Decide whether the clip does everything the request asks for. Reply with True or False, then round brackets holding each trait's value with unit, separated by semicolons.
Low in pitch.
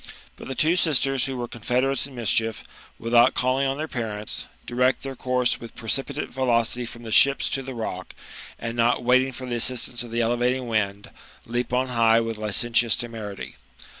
True (120 Hz)